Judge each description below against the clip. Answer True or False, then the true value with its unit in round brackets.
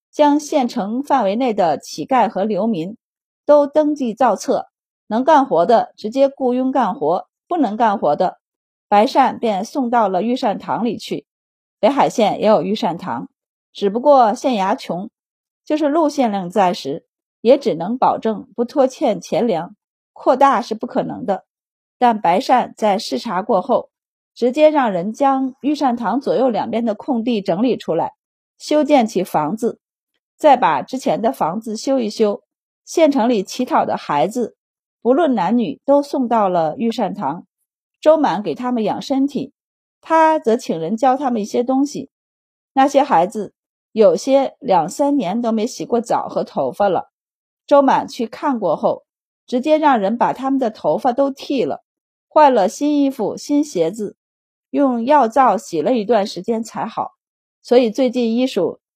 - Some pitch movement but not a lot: True (4.1 semitones)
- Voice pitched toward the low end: False (250 Hz)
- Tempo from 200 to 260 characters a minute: True (225 characters per minute)